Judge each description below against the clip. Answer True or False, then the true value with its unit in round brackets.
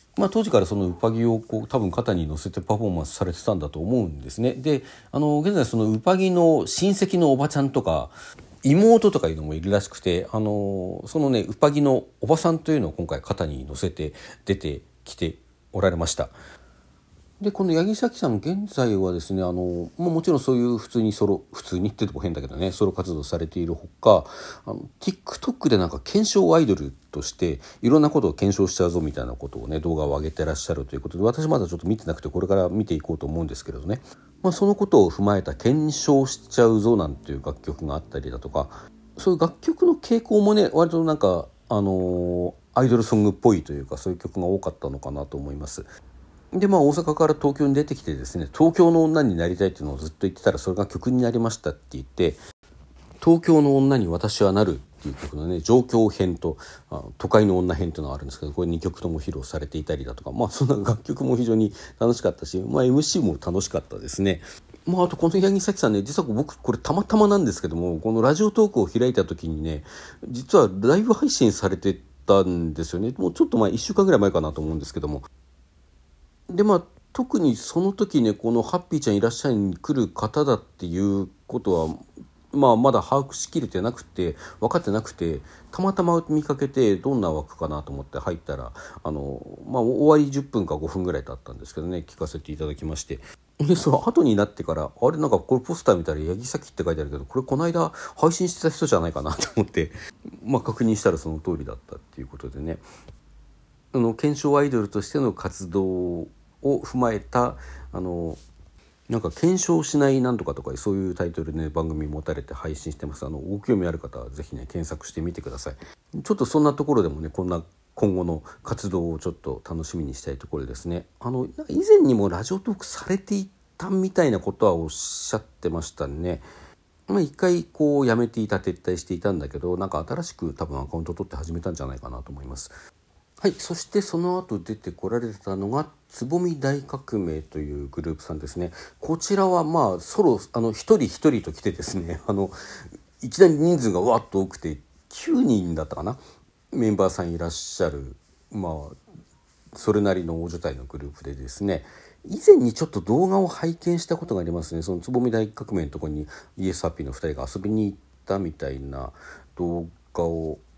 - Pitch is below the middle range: True (95 Hz)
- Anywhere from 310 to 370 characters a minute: False (415 characters per minute)